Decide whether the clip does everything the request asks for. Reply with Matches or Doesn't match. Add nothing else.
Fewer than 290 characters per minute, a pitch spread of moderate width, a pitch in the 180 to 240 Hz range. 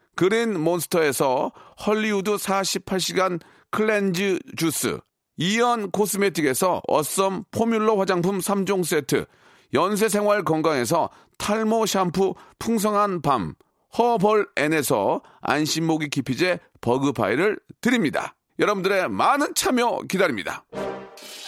Matches